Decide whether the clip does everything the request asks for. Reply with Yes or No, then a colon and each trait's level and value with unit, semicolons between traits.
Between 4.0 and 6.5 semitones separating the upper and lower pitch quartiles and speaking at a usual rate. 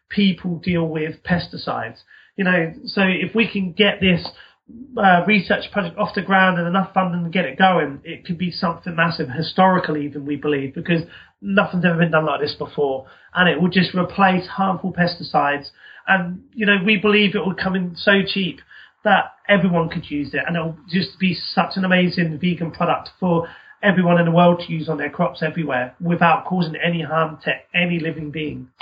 No: average, 2.9 semitones; average, 195 wpm